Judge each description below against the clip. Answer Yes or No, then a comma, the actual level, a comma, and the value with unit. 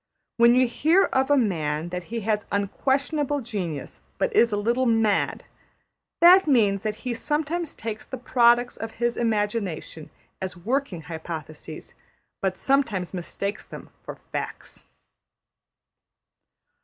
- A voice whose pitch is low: No, high, 225 Hz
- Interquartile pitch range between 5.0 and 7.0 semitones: Yes, wide, 5.6 semitones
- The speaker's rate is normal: No, slow, 130 wpm